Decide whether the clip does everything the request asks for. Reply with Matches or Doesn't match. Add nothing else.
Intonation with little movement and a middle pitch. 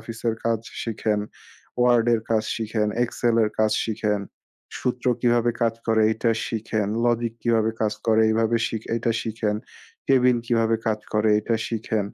Doesn't match